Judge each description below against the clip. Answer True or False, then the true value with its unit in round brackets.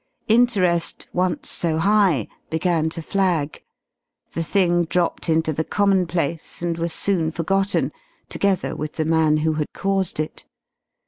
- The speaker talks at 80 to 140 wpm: True (135 wpm)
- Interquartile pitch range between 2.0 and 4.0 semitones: True (3.0 semitones)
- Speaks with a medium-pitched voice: True (170 Hz)